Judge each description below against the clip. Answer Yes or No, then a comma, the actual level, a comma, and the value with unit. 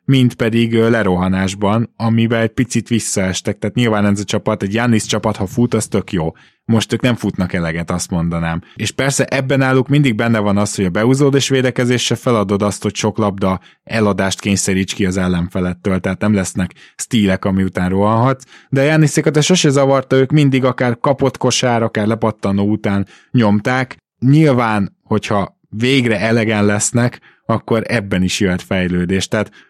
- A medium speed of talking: No, fast, 170 wpm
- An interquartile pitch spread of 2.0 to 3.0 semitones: No, average, 4.1 semitones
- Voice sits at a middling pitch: No, low, 110 Hz